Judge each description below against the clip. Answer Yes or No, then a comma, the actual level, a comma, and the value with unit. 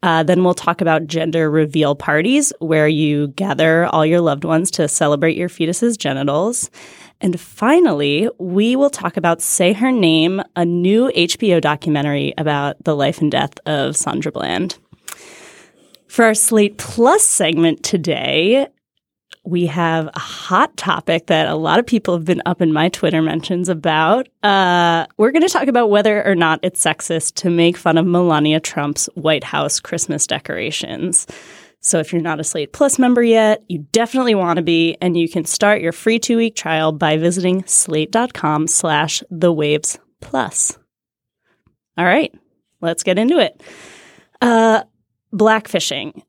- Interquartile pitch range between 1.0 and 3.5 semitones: No, average, 5.1 semitones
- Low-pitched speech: No, medium, 175 Hz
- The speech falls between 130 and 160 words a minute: Yes, average, 155 wpm